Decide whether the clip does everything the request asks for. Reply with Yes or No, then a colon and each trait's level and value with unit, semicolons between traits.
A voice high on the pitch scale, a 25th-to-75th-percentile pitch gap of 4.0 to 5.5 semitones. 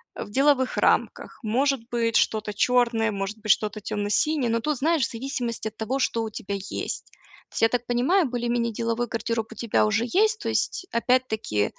No: high, 230 Hz; average, 2.8 semitones